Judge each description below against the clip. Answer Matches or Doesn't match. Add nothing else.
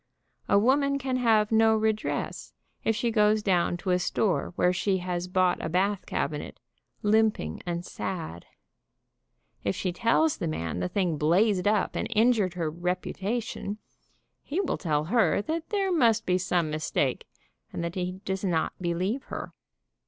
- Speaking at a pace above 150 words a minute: Matches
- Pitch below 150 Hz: Doesn't match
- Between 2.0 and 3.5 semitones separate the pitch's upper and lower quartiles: Doesn't match